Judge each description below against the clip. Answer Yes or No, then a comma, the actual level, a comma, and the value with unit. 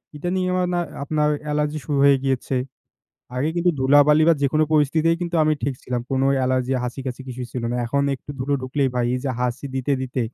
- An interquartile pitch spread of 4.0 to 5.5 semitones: No, average, 2.8 semitones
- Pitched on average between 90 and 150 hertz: Yes, medium, 140 Hz